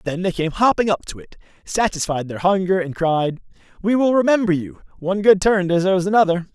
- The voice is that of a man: Yes, male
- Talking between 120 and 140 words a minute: No, average, 185 wpm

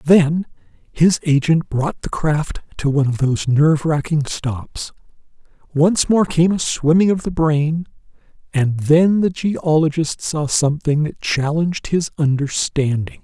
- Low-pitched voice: No, medium, 155 Hz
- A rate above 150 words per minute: No, average, 140 wpm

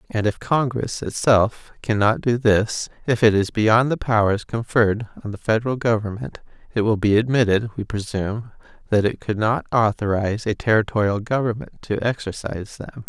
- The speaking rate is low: No, average, 155 wpm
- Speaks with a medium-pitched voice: No, low, 110 Hz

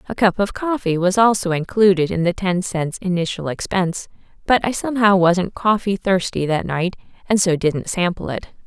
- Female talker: Yes, female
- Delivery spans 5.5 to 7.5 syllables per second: No, 5.1 syllables/s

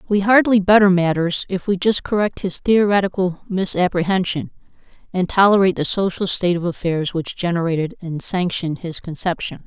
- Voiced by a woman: Yes, female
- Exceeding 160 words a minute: No, average, 150 wpm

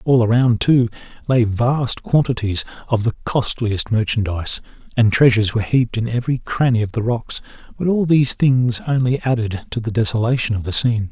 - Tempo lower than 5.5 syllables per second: No, 5.6 syllables/s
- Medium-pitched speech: No, low, 115 Hz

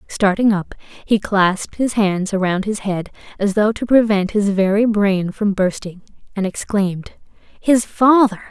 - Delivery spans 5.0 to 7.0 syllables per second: No, 4.4 syllables/s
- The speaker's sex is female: Yes, female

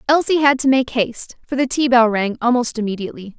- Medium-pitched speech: No, high, 245 Hz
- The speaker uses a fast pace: Yes, fast, 215 wpm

